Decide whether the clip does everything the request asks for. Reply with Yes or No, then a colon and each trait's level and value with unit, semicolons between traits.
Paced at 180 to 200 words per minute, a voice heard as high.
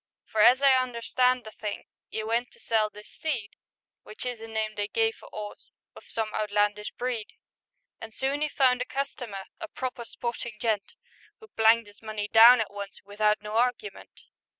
Yes: average, 190 wpm; high, 225 Hz